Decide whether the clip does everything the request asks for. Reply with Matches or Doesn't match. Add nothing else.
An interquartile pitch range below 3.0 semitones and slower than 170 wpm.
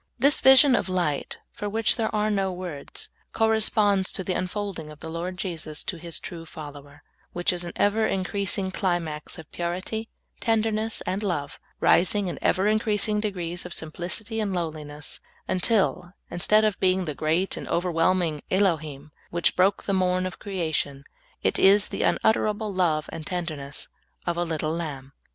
Doesn't match